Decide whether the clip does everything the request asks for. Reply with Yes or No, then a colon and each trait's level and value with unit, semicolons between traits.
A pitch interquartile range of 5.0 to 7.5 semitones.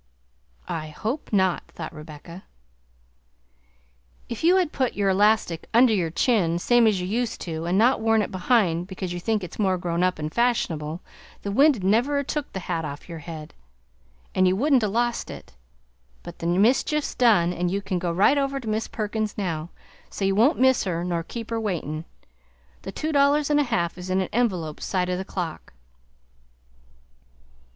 Yes: wide, 5.4 semitones